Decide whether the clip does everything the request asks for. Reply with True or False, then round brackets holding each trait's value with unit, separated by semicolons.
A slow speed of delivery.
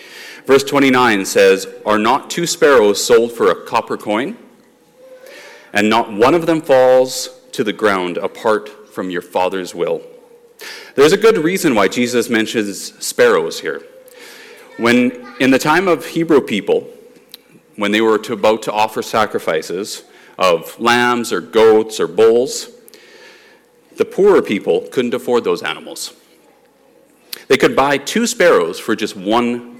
False (145 wpm)